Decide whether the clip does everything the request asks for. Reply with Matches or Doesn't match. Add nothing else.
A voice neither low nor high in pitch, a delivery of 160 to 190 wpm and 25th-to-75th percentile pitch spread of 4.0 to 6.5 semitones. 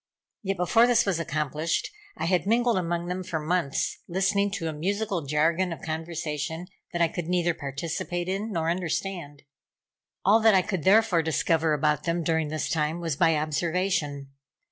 Doesn't match